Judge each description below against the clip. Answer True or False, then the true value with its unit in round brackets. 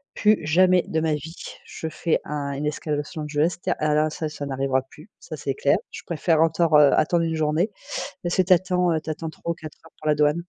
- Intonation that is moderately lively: False (2.1 semitones)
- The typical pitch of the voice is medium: True (155 Hz)